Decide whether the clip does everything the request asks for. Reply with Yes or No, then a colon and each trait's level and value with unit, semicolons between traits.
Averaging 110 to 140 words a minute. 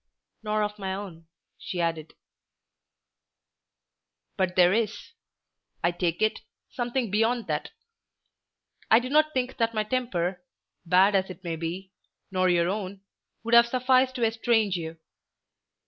Yes: slow, 135 wpm